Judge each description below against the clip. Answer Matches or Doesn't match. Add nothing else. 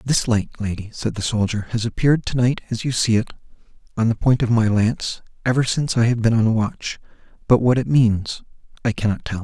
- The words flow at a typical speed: Doesn't match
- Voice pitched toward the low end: Matches